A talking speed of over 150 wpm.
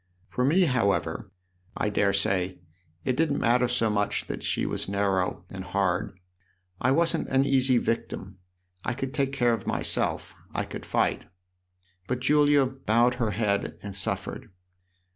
No: average, 145 wpm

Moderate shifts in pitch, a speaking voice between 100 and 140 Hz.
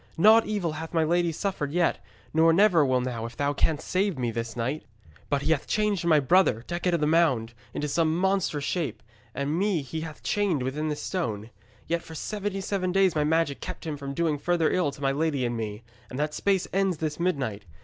No: average, 4.3 semitones; medium, 160 Hz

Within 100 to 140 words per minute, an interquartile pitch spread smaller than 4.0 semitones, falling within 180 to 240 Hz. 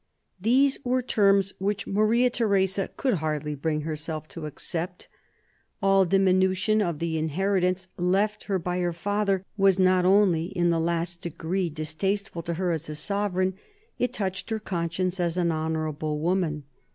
No: average, 155 wpm; average, 3.2 semitones; medium, 185 Hz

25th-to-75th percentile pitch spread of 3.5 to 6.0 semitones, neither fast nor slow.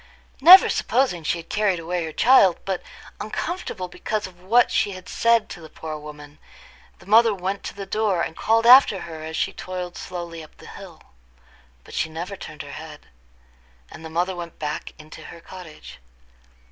Yes: average, 4.4 semitones; average, 185 wpm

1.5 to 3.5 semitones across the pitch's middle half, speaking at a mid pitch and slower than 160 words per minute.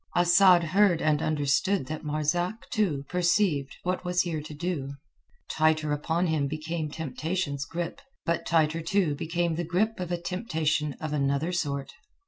Yes: average, 2.9 semitones; medium, 160 Hz; average, 150 wpm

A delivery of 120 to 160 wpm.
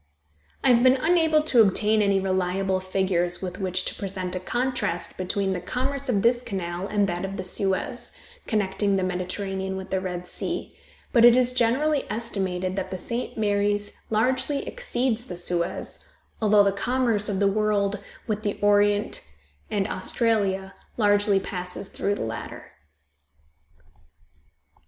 Yes: average, 150 wpm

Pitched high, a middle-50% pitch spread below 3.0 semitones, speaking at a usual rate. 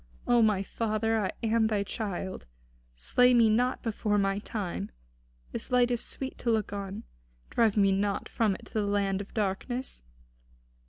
Yes: high, 215 Hz; narrow, 2.6 semitones; average, 165 wpm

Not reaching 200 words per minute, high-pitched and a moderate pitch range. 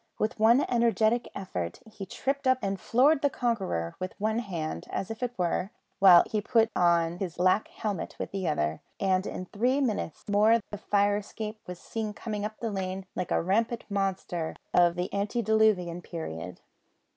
Yes: average, 170 wpm; high, 200 Hz; average, 3.7 semitones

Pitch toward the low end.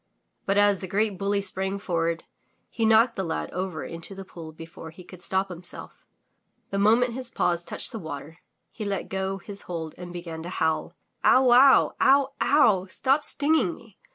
No: high, 190 Hz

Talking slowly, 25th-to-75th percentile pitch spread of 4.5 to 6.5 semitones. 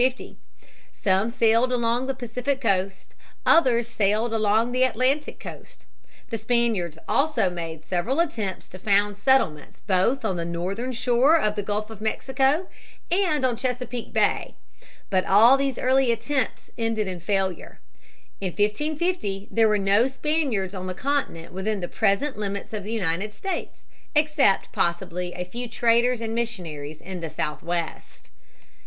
No: average, 145 wpm; average, 5.0 semitones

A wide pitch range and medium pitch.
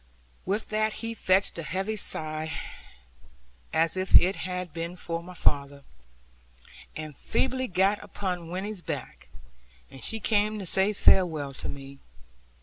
No: average, 4.4 semitones; medium, 180 Hz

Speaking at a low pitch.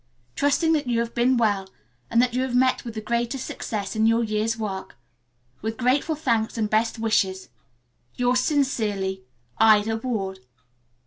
No: high, 230 Hz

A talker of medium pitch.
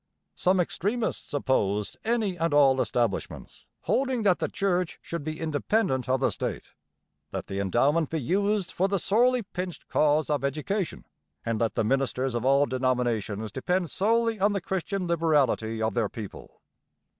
Yes: medium, 155 Hz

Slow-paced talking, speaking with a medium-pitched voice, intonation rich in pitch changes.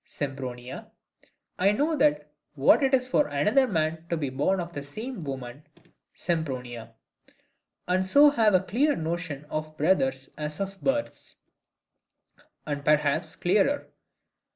Yes: slow, 130 wpm; medium, 160 Hz; wide, 6.7 semitones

